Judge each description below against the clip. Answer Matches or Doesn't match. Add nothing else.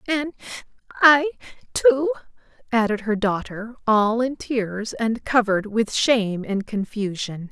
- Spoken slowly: Matches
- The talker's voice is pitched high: Matches